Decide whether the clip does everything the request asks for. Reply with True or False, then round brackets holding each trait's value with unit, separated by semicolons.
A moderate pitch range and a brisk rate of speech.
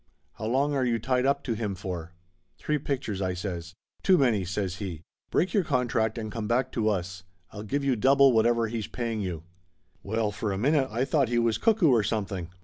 True (4.9 semitones; 215 wpm)